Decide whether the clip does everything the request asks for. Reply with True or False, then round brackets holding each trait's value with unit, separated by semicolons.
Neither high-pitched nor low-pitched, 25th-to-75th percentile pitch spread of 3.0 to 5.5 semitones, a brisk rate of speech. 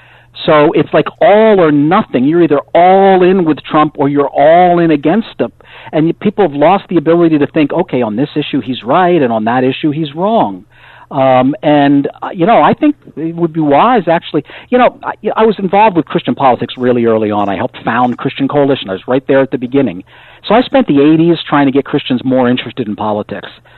True (150 Hz; 4.9 semitones; 220 wpm)